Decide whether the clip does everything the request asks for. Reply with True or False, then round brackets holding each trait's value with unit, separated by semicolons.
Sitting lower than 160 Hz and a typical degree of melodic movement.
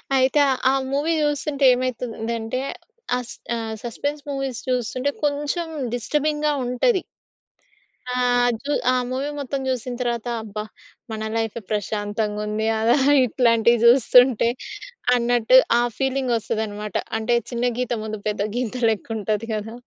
False (245 Hz; 3.1 semitones)